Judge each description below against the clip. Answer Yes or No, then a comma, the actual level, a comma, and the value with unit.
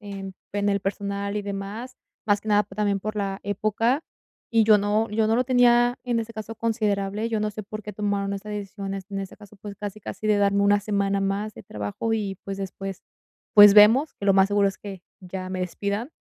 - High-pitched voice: Yes, high, 205 Hz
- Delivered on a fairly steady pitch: Yes, narrow, 1.5 semitones